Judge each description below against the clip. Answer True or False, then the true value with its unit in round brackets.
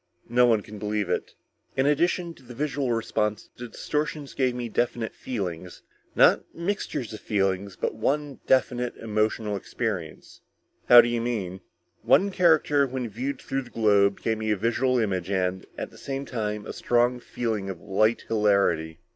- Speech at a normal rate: True (165 wpm)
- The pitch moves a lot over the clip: False (3.9 semitones)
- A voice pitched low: True (115 Hz)